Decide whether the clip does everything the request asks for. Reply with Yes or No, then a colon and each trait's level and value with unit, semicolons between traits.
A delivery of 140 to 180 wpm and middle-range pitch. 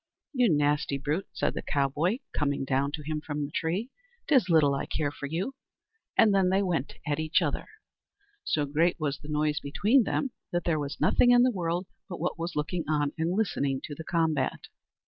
No: average, 200 wpm; medium, 155 Hz